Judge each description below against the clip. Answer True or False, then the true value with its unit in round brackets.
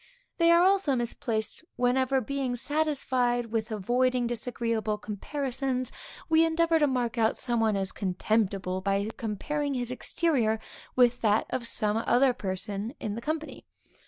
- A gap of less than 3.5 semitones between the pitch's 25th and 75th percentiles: False (3.9 semitones)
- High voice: True (240 Hz)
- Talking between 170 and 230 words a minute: False (140 wpm)